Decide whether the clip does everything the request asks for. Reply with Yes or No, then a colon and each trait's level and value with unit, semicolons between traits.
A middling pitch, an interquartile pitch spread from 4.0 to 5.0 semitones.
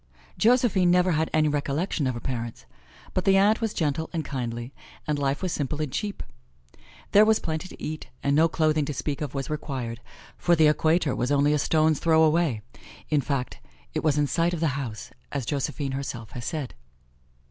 No: medium, 150 Hz; average, 3.3 semitones